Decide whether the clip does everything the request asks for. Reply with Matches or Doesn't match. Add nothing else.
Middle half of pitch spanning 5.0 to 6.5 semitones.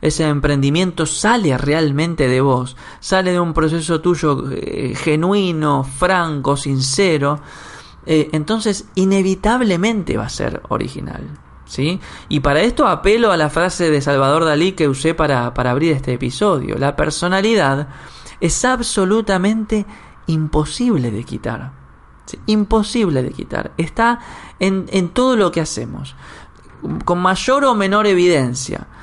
Matches